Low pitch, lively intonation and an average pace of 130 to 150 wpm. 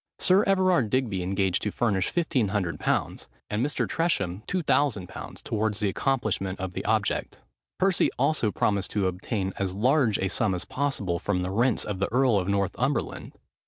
No: low, 105 Hz; wide, 5.7 semitones; average, 160 wpm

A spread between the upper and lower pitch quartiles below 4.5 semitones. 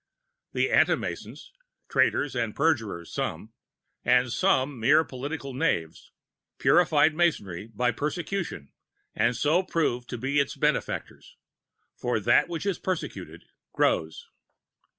No: wide, 5.6 semitones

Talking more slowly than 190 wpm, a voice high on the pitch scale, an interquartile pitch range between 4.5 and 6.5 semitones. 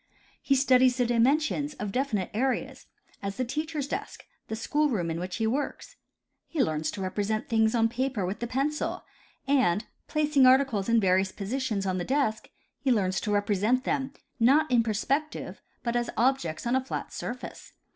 Yes: average, 175 wpm; high, 240 Hz; average, 4.8 semitones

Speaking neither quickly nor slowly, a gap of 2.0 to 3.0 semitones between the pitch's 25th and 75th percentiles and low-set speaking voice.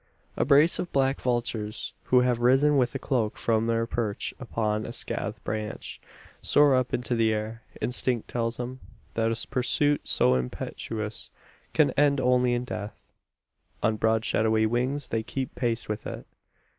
Yes: average, 160 wpm; narrow, 2.6 semitones; low, 120 Hz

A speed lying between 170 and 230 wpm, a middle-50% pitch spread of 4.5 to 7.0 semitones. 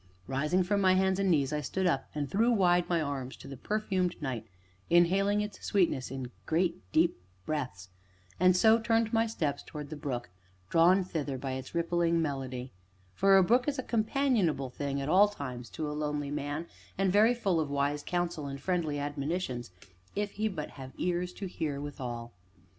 Yes: average, 185 wpm; average, 5.2 semitones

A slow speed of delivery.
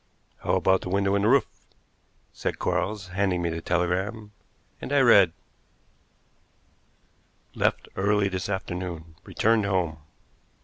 Yes: slow, 125 wpm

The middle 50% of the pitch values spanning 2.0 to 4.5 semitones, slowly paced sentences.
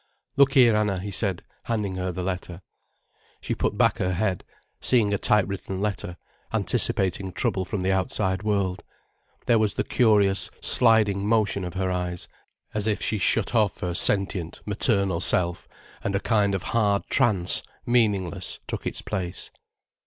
No: narrow, 2.5 semitones; average, 155 wpm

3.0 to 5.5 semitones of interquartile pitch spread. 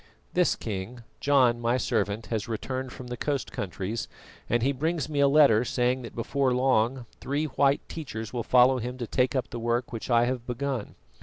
No: narrow, 2.5 semitones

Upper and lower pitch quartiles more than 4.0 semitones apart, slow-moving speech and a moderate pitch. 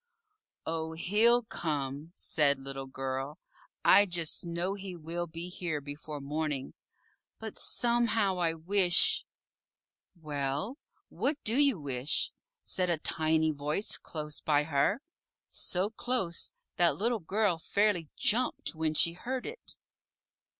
Yes: average, 5.2 semitones; slow, 125 wpm; medium, 170 Hz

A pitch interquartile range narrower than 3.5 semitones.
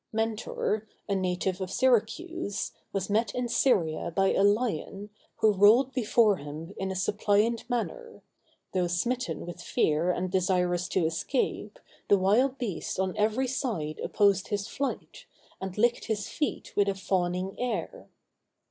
No: average, 4.2 semitones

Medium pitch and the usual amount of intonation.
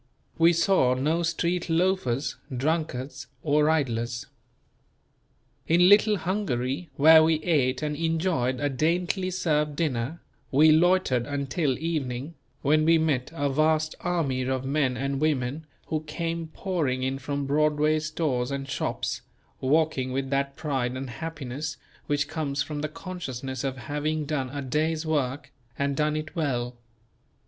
Yes: medium, 150 Hz; average, 3.4 semitones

